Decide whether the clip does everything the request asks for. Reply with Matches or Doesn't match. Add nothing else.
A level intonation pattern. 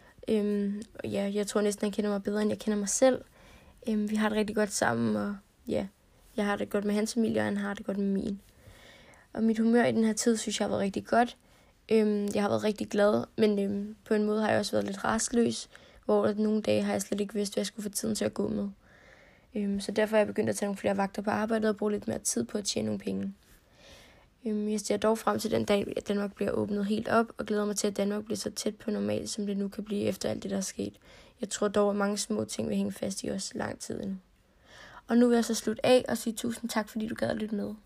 Matches